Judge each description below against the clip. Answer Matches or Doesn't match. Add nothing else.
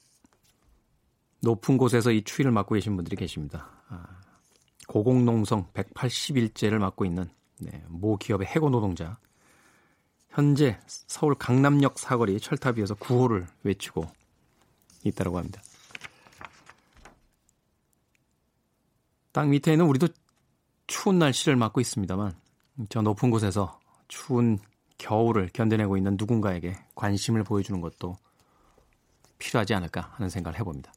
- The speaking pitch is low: Matches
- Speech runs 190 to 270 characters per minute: Matches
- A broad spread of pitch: Doesn't match